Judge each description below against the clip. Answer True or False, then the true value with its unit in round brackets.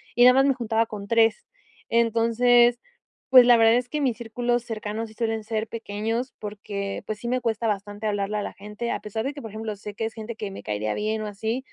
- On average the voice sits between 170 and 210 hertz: False (225 Hz)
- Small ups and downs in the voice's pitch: True (2.2 semitones)